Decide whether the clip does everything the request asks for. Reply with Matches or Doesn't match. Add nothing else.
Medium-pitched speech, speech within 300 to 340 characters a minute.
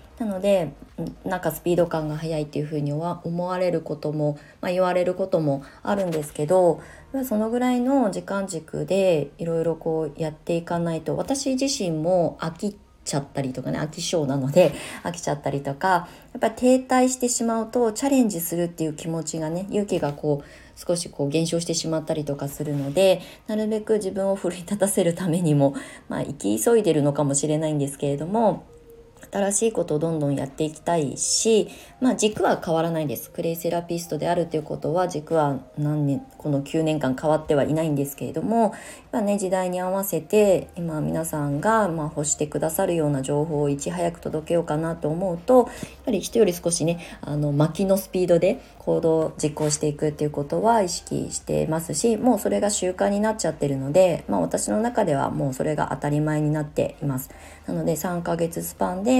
Doesn't match